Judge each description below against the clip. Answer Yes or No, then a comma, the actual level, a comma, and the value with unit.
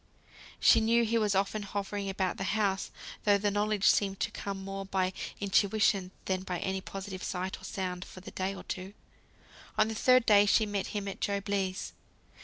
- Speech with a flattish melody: Yes, narrow, 1.4 semitones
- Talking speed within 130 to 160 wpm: No, average, 200 wpm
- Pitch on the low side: No, high, 195 Hz